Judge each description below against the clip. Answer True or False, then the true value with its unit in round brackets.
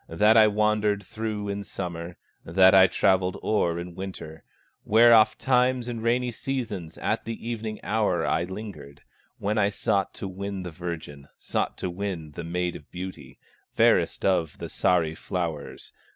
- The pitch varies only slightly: False (3.7 semitones)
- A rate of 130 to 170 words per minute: True (155 wpm)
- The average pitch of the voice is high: False (95 Hz)